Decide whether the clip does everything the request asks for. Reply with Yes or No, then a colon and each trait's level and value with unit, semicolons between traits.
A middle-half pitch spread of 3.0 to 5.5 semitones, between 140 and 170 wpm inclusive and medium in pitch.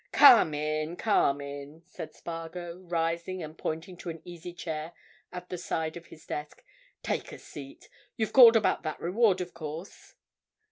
No: narrow, 2.5 semitones; average, 160 wpm; medium, 170 Hz